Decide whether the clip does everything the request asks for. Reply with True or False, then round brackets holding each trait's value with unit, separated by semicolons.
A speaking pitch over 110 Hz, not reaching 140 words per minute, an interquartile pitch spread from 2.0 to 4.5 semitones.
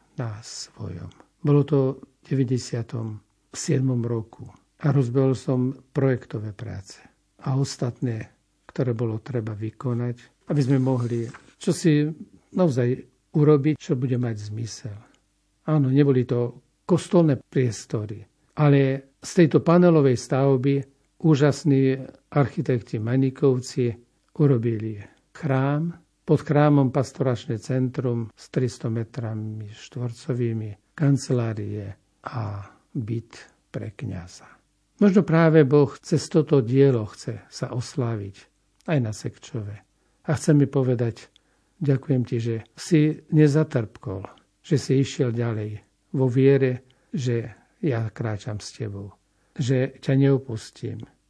True (130 Hz; 110 wpm; 3.8 semitones)